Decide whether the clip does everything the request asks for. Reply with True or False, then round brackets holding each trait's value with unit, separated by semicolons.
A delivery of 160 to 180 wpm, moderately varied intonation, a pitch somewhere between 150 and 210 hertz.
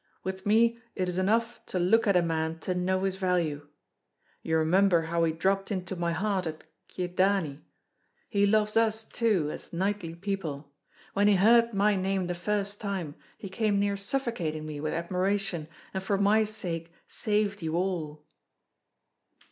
True (165 wpm; 3.3 semitones; 190 Hz)